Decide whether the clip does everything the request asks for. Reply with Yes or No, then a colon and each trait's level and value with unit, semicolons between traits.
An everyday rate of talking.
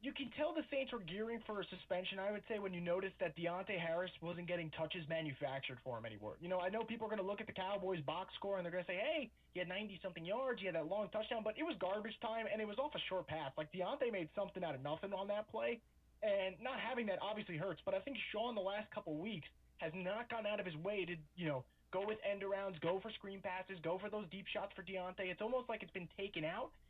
No: fast, 275 wpm